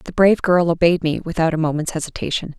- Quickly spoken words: Yes, fast, 210 wpm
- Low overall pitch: No, medium, 165 Hz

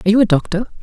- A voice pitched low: No, high, 205 Hz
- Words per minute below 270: No, fast, 290 wpm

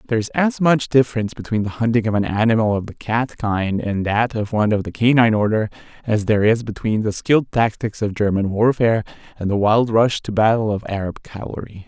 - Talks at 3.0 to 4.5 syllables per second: No, 5.9 syllables/s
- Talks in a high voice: No, low, 110 Hz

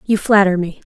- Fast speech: No, average, 195 wpm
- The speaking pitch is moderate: No, high, 195 Hz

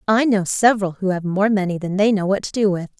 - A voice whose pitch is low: No, high, 200 Hz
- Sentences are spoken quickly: Yes, fast, 280 wpm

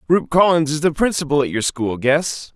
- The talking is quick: Yes, fast, 210 wpm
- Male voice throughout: Yes, male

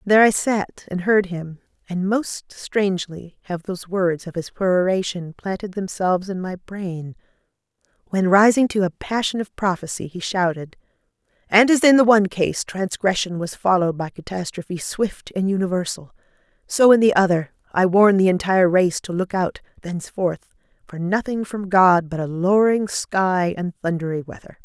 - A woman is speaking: Yes, female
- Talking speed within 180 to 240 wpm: No, average, 165 wpm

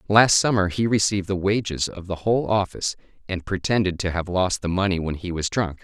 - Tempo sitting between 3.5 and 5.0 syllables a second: No, 5.9 syllables/s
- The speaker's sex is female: No, male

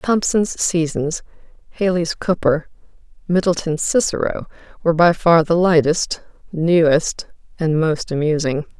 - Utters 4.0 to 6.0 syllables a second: Yes, 4.2 syllables/s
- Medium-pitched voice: Yes, medium, 165 Hz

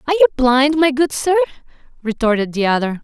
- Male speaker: No, female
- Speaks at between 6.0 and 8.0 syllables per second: Yes, 6.3 syllables/s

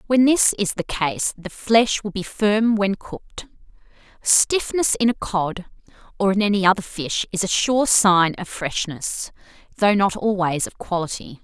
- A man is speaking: No, female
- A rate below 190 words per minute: Yes, average, 170 wpm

